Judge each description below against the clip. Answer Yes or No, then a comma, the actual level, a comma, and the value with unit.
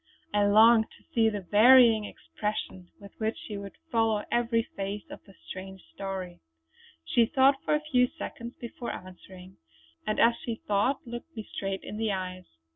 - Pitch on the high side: Yes, high, 215 Hz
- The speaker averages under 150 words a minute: No, average, 170 wpm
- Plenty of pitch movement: No, average, 3.2 semitones